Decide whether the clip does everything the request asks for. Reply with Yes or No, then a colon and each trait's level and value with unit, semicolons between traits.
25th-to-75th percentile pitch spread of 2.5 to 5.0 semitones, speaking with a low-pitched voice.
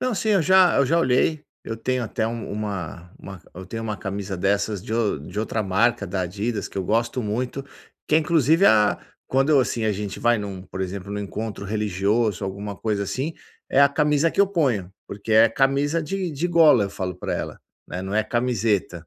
No: wide, 5.5 semitones; low, 110 Hz